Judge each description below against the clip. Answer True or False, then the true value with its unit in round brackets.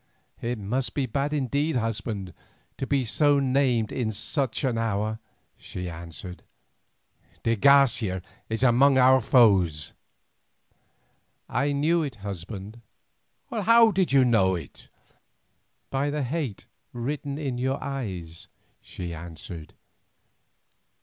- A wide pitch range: True (5.7 semitones)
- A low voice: True (120 Hz)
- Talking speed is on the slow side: True (115 wpm)